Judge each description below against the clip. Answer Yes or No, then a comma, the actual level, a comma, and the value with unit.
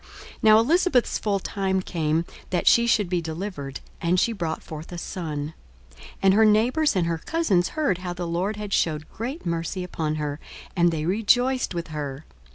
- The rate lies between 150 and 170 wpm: No, average, 185 wpm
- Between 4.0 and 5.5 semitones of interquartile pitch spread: Yes, average, 4.9 semitones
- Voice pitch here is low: No, medium, 180 Hz